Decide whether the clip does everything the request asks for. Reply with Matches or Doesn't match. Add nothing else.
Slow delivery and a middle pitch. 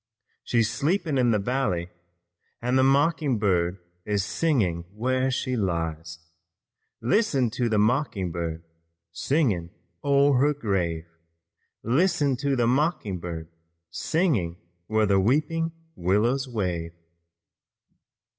Doesn't match